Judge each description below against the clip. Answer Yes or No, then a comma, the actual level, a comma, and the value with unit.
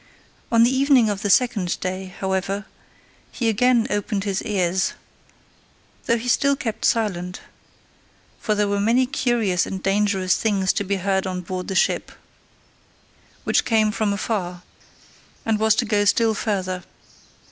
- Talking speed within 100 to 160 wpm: Yes, average, 145 wpm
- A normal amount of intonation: Yes, average, 3.0 semitones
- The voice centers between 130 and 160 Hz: No, high, 205 Hz